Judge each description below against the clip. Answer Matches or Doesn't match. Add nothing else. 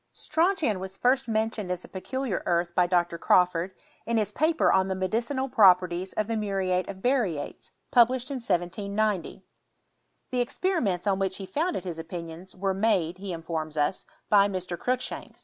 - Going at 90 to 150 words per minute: Doesn't match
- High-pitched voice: Matches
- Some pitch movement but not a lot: Matches